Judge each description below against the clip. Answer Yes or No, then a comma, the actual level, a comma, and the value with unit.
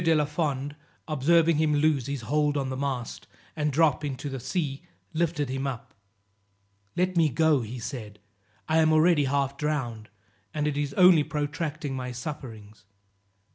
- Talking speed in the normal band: Yes, average, 160 wpm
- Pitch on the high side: No, medium, 145 Hz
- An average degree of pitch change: Yes, average, 3.1 semitones